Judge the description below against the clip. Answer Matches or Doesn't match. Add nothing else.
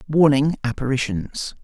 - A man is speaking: Matches